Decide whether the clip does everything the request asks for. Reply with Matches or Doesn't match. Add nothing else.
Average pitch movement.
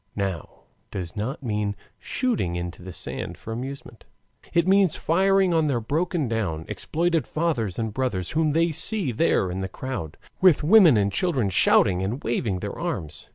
Doesn't match